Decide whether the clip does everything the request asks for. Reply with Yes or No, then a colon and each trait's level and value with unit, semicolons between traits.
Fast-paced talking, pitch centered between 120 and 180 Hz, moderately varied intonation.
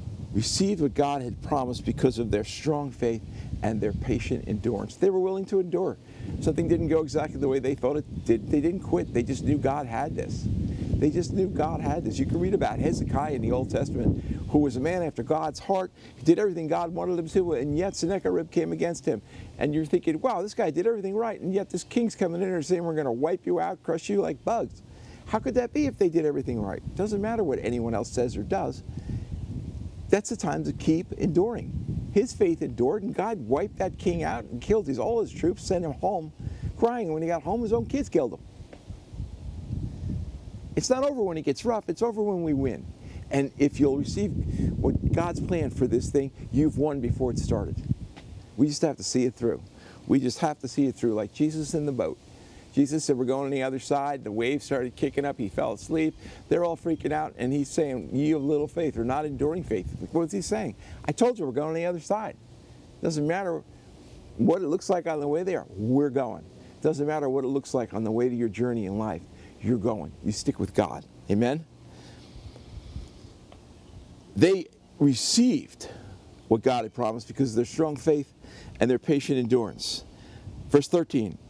No: fast, 215 wpm; medium, 140 Hz; wide, 6.3 semitones